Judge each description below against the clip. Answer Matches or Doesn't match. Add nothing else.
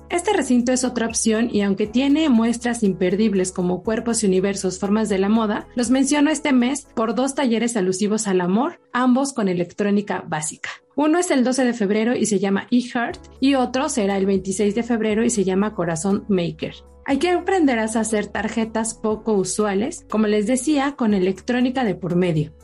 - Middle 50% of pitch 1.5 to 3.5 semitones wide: Doesn't match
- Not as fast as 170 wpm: Doesn't match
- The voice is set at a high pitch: Matches